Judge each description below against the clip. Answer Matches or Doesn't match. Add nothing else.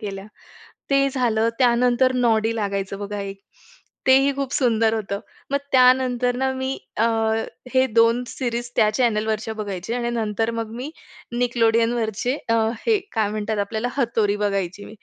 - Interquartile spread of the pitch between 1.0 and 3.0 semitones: Matches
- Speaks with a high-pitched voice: Matches